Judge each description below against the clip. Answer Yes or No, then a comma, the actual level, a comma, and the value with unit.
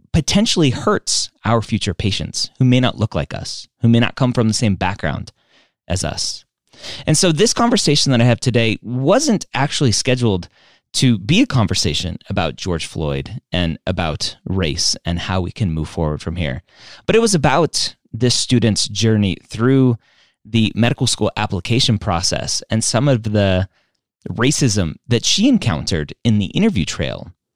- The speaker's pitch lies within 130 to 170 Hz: No, low, 115 Hz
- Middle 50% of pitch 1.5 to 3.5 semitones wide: No, average, 5.2 semitones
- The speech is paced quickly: No, average, 165 wpm